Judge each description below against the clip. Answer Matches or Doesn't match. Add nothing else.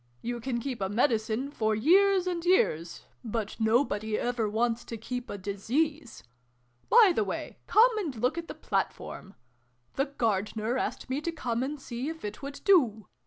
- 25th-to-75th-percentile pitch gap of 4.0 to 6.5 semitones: Matches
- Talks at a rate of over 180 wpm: Doesn't match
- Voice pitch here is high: Matches